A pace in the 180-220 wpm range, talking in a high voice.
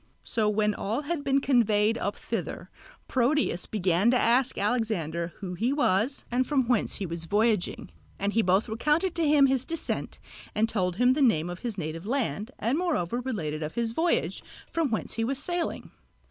Yes: average, 185 wpm; high, 225 Hz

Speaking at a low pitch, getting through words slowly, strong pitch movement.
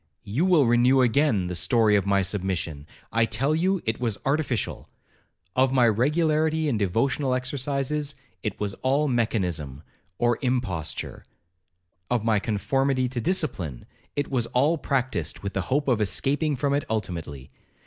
Yes: low, 120 Hz; slow, 130 wpm; wide, 6.1 semitones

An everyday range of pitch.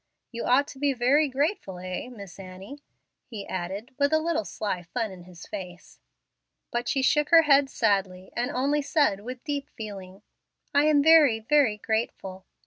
No: wide, 6.7 semitones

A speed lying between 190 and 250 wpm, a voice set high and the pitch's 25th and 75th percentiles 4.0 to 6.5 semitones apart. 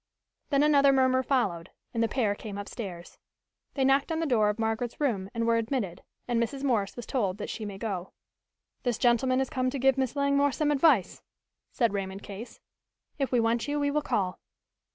Yes: average, 195 wpm; high, 240 Hz; average, 4.7 semitones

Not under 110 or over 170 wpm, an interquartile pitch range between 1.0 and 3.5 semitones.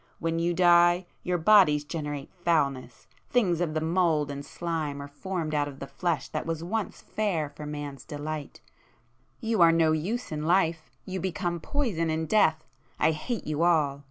Yes: average, 155 wpm; average, 3.0 semitones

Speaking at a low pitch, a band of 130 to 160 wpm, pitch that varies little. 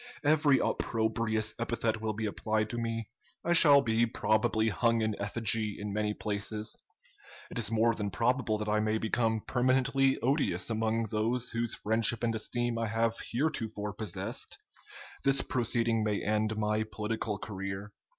Yes: low, 110 Hz; average, 150 wpm; narrow, 1.6 semitones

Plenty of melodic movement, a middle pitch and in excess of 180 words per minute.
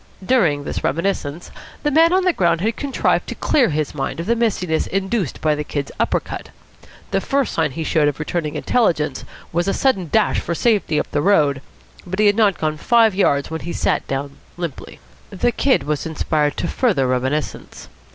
Yes: wide, 6.7 semitones; medium, 170 Hz; average, 195 wpm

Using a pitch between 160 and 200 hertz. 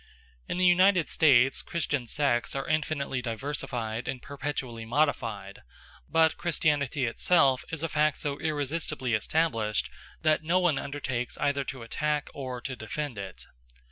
No: medium, 140 Hz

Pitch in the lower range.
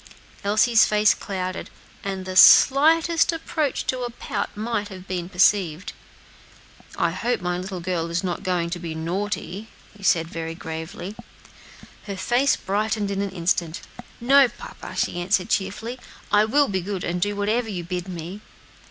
No: high, 195 Hz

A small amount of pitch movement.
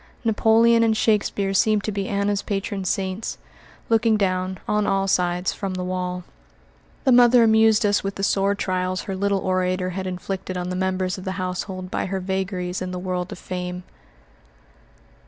Yes: narrow, 1.9 semitones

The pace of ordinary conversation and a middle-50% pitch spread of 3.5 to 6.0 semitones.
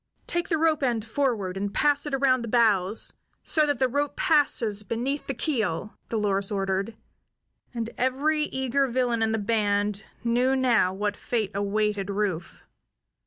Yes: average, 155 wpm; average, 4.7 semitones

